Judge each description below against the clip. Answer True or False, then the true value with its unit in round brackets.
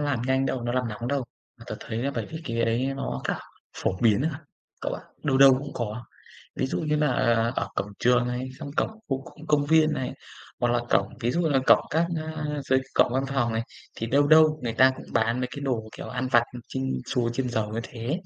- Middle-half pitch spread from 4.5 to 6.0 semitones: False (3.4 semitones)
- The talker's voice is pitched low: True (130 Hz)